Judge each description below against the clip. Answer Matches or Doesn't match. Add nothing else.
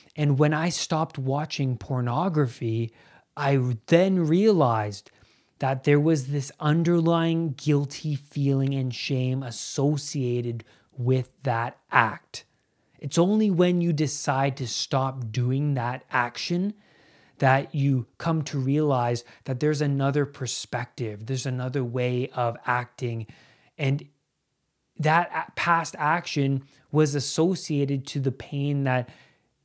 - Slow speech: Matches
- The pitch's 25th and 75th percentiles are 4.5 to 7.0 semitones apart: Doesn't match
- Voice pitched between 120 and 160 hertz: Matches